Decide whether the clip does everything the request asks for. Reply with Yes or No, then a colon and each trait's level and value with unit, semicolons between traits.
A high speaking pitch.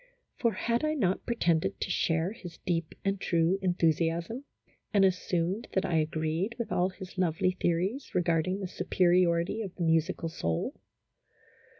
No: medium, 180 Hz